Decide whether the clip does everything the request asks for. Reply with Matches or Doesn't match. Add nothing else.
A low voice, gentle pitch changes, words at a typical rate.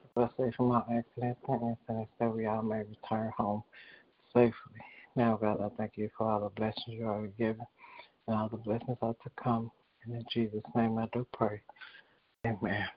Matches